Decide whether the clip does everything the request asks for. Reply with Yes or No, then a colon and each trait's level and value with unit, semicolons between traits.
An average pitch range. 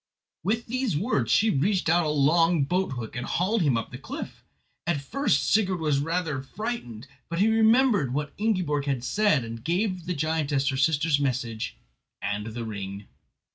No: wide, 6.3 semitones